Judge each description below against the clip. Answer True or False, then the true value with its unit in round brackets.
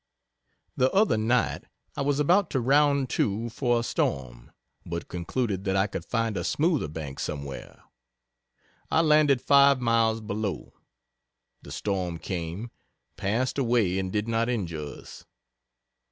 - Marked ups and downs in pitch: True (6.1 semitones)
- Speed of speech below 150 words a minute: True (140 wpm)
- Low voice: True (115 Hz)